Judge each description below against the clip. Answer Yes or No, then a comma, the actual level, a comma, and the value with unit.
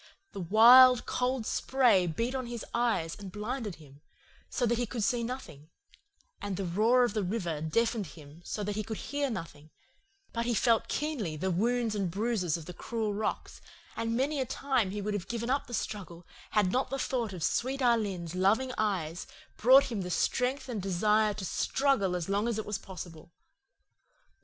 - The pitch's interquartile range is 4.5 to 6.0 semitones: Yes, average, 4.8 semitones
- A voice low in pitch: No, high, 215 Hz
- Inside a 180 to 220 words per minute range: Yes, average, 190 wpm